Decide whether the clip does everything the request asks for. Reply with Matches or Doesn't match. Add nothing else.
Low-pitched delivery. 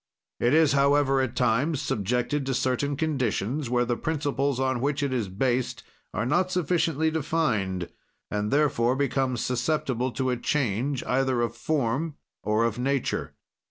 Matches